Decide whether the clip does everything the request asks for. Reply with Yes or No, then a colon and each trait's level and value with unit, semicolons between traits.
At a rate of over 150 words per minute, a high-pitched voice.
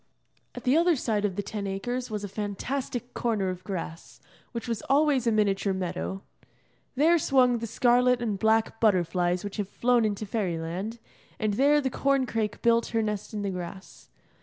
Yes: average, 180 wpm; high, 220 Hz